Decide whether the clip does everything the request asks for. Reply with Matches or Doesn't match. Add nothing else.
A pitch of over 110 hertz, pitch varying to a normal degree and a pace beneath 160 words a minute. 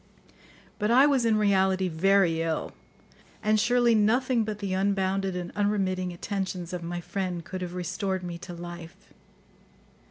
Matches